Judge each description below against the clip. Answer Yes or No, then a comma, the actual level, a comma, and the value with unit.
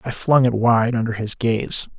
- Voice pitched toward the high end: No, low, 115 Hz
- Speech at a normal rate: No, fast, 210 wpm